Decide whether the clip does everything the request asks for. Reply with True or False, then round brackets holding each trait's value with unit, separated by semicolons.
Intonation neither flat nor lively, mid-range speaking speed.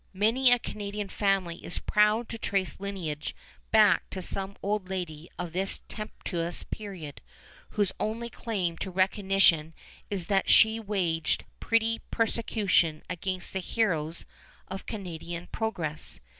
False (3.6 semitones; 130 wpm)